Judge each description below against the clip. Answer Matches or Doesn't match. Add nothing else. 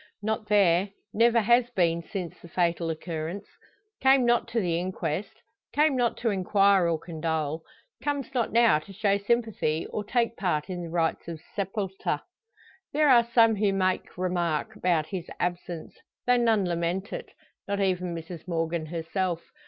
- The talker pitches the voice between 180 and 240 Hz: Matches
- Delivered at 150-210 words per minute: Matches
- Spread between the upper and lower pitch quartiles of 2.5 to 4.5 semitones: Doesn't match